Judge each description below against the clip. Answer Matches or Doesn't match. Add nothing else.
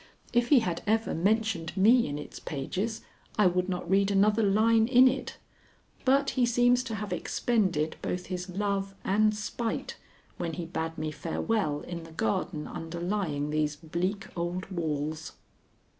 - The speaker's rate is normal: Matches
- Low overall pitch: Doesn't match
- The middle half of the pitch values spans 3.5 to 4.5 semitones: Doesn't match